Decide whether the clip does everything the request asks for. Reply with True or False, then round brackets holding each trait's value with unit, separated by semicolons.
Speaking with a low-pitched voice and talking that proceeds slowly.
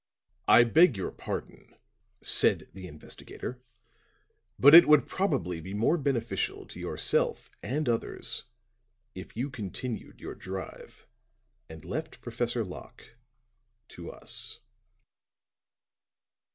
True (120 Hz; 105 wpm)